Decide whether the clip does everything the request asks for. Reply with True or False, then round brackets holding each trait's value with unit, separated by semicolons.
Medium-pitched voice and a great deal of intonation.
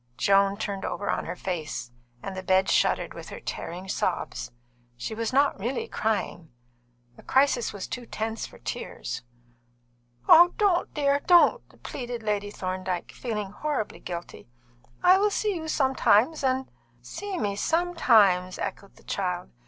False (215 Hz; 6.9 semitones)